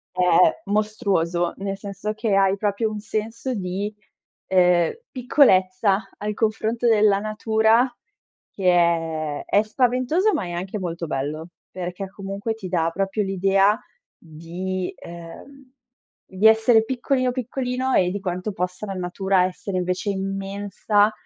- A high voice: Yes, high, 195 Hz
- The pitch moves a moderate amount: Yes, average, 3.2 semitones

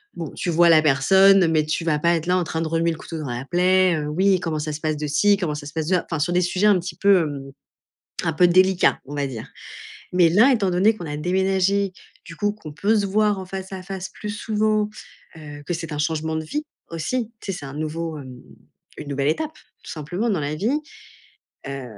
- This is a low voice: No, medium, 170 Hz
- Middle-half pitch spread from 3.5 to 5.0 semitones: Yes, average, 4.0 semitones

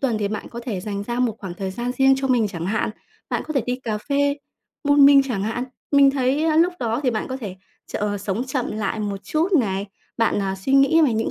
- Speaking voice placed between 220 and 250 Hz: Yes, high, 240 Hz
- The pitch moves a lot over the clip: No, average, 4.8 semitones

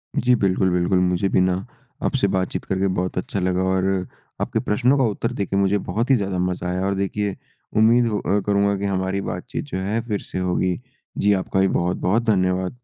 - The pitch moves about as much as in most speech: No, narrow, 2.0 semitones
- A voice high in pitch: No, very low, 95 Hz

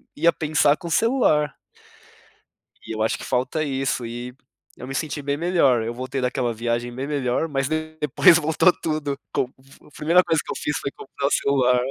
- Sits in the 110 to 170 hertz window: Yes, medium, 140 Hz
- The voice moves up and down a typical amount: Yes, average, 3.7 semitones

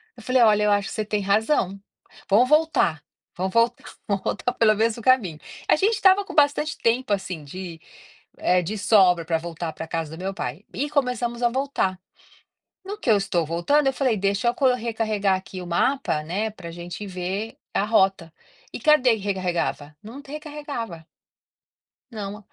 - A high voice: Yes, high, 210 Hz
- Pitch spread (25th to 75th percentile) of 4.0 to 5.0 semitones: No, wide, 5.6 semitones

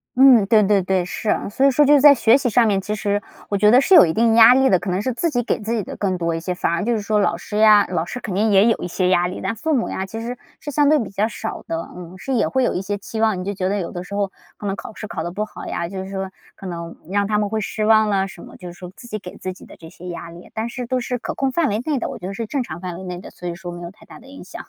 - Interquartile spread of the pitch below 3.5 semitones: No, average, 4.2 semitones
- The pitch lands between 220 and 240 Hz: No, high, 205 Hz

